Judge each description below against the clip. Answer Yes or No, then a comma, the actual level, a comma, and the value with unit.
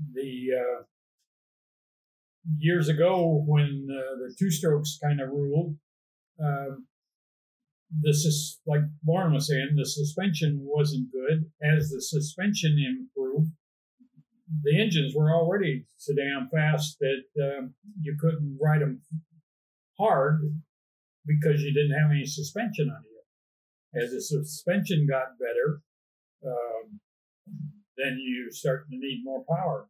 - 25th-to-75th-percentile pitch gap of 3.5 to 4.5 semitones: No, average, 2.7 semitones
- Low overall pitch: No, medium, 150 Hz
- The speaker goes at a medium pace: No, slow, 125 wpm